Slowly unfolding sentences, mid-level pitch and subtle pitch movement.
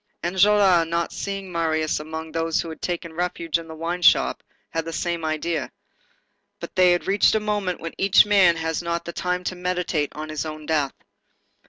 No: average, 190 wpm; medium, 170 Hz; narrow, 2.1 semitones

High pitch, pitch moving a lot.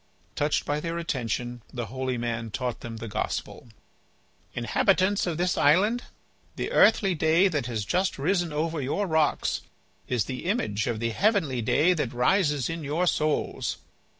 No: medium, 150 Hz; wide, 6.5 semitones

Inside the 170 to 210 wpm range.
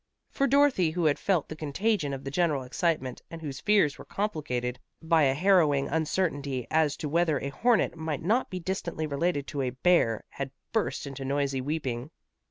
Yes: average, 180 wpm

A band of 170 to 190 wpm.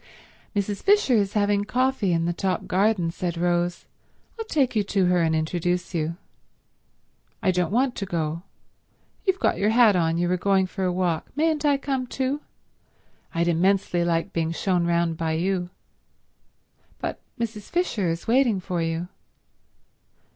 No: average, 160 wpm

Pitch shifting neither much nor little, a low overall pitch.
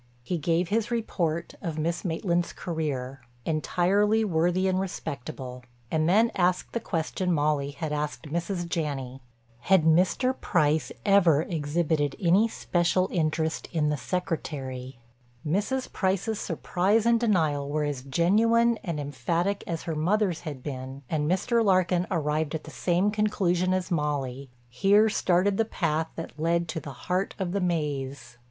No: average, 4.2 semitones; medium, 170 Hz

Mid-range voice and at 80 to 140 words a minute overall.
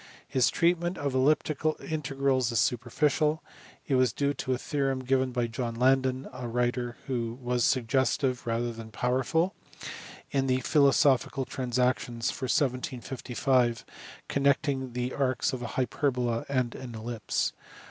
No: low, 130 Hz; slow, 135 wpm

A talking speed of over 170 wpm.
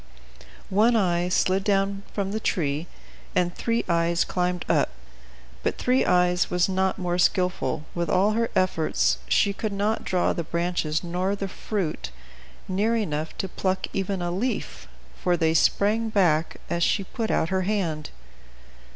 No: average, 155 wpm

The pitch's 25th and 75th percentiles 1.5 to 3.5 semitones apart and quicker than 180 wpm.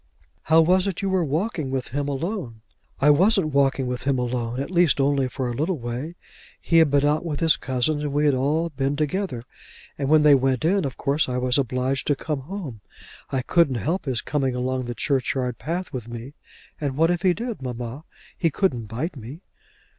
No: average, 4.2 semitones; fast, 205 wpm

